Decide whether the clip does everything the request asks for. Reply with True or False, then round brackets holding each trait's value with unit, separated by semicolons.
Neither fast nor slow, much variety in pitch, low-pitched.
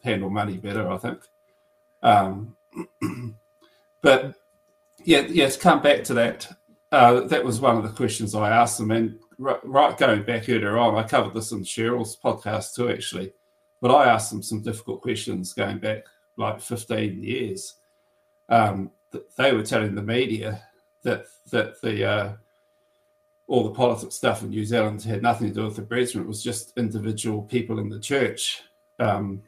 True (170 wpm; 6.0 semitones; 115 Hz)